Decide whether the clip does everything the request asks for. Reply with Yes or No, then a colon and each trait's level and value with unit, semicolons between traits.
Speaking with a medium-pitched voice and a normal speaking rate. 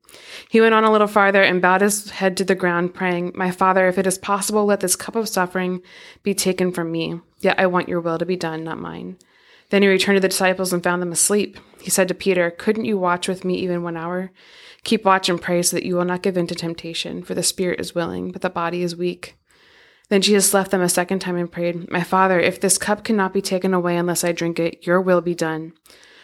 No: medium, 180 Hz; fast, 250 wpm